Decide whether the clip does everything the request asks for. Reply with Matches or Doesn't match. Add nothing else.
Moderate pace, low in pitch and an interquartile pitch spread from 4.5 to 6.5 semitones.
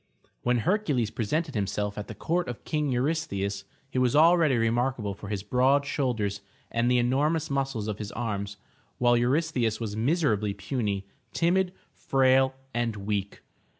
Matches